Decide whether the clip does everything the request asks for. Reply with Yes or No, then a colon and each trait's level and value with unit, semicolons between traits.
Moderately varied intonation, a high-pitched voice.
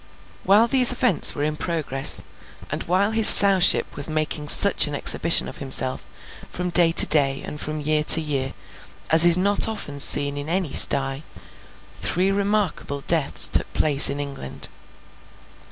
No: average, 4.9 semitones; medium, 155 Hz